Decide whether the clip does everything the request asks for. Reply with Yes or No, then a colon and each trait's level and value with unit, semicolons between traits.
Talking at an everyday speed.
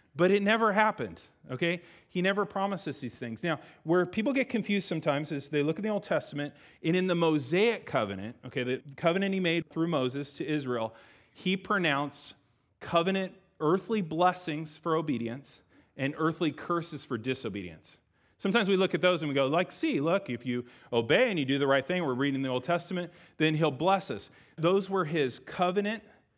Yes: average, 185 wpm